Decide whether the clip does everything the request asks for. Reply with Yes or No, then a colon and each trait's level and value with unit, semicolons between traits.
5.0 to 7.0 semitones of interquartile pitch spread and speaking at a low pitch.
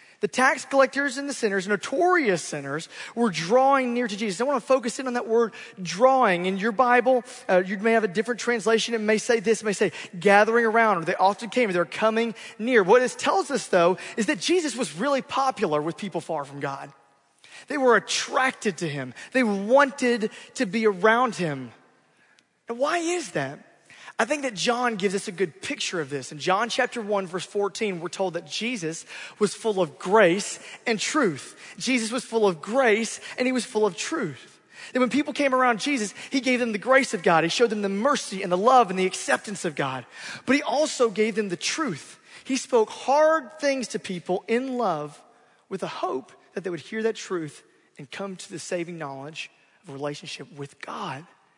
No: wide, 5.5 semitones; high, 220 Hz